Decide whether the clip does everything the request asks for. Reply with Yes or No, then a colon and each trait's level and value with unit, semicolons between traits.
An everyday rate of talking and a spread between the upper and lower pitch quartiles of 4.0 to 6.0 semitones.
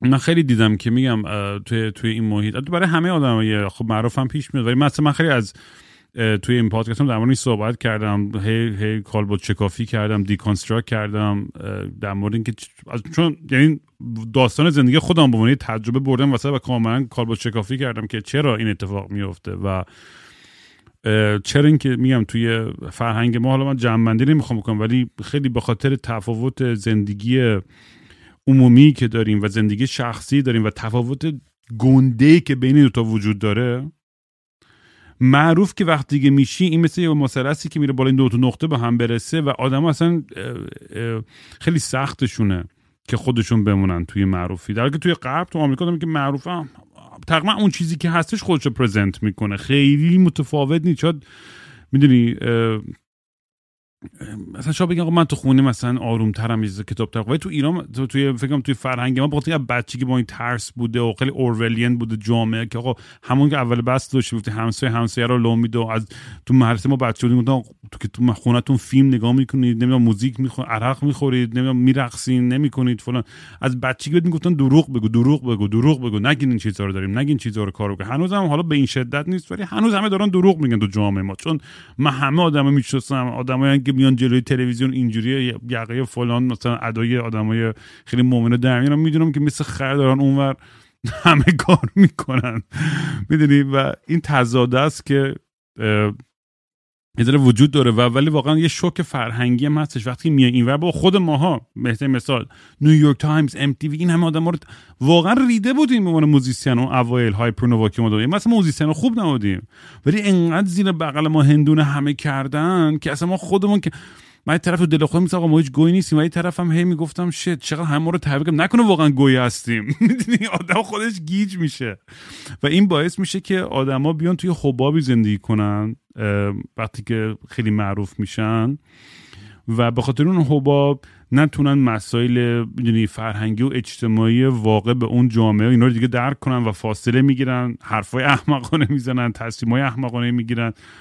No: fast, 175 wpm; average, 4.5 semitones